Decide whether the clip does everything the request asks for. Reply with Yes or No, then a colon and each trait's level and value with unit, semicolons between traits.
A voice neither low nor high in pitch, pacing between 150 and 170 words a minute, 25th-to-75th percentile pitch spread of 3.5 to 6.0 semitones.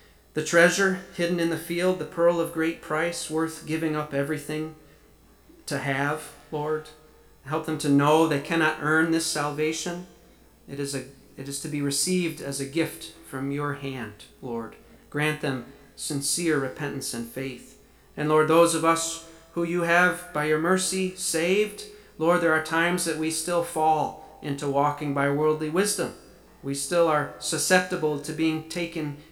No: medium, 155 Hz; average, 165 wpm; narrow, 2.6 semitones